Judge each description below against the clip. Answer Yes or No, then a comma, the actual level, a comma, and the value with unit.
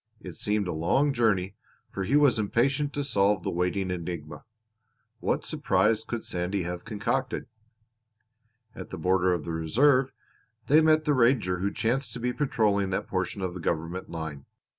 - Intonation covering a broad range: Yes, wide, 5.9 semitones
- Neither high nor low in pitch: No, low, 100 Hz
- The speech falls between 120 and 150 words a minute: No, average, 165 wpm